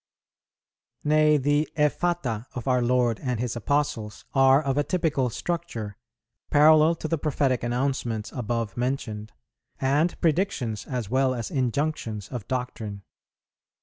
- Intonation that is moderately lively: Yes, average, 4.2 semitones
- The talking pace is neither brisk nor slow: No, slow, 125 wpm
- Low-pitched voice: Yes, low, 130 Hz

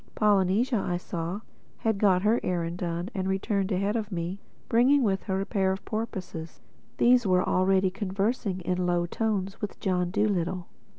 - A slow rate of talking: No, average, 165 wpm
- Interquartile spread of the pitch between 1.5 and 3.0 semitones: Yes, narrow, 2.6 semitones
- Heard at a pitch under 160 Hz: No, high, 190 Hz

